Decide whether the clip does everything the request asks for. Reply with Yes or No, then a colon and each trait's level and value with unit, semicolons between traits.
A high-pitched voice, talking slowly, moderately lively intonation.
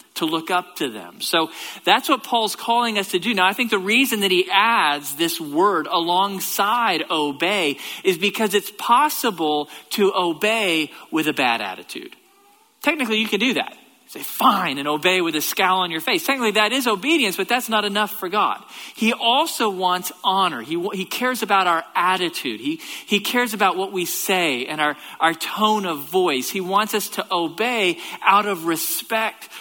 No: high, 200 Hz; average, 185 wpm; average, 4.9 semitones